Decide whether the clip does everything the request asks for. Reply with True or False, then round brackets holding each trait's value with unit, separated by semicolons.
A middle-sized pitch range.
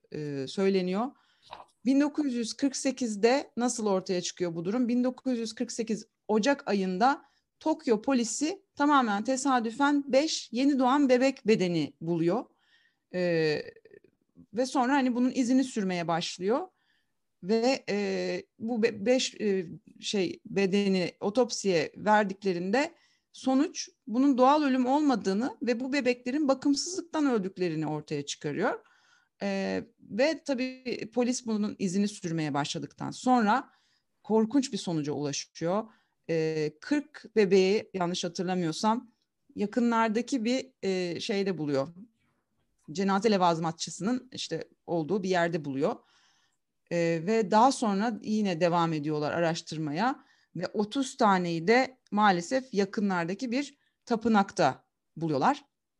False (6.3 semitones)